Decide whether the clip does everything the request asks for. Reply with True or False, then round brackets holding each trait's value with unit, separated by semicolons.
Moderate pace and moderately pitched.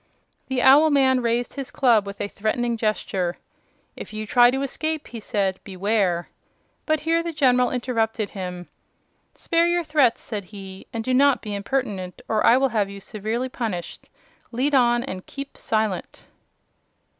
False (165 wpm; 235 Hz)